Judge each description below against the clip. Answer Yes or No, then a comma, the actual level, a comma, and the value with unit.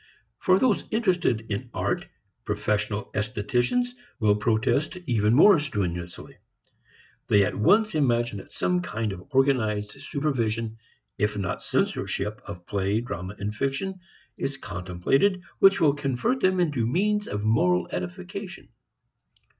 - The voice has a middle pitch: No, low, 115 Hz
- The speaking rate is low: Yes, slow, 125 wpm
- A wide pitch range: Yes, wide, 6.6 semitones